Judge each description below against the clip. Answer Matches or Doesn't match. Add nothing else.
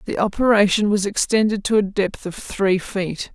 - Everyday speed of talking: Matches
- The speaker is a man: Doesn't match